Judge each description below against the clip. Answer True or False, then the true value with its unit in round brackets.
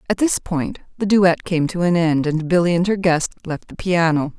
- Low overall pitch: False (170 Hz)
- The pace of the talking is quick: True (235 wpm)